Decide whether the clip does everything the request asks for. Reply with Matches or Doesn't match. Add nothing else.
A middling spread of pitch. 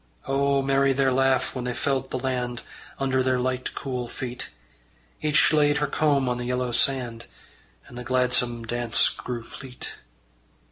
Doesn't match